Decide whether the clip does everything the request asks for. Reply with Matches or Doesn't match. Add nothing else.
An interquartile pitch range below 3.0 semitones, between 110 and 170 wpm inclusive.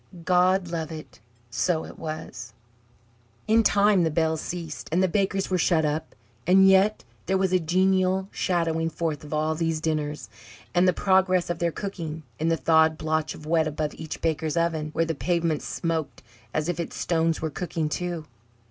Doesn't match